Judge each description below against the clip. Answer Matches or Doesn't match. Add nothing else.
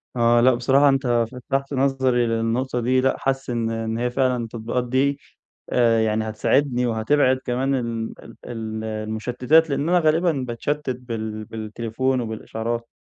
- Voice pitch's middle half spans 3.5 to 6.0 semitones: Doesn't match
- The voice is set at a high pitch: Doesn't match